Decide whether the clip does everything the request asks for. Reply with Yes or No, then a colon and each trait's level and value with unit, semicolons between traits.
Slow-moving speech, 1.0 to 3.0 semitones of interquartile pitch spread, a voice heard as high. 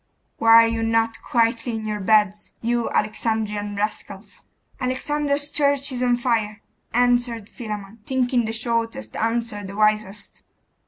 Yes: slow, 130 wpm; narrow, 2.4 semitones; high, 225 Hz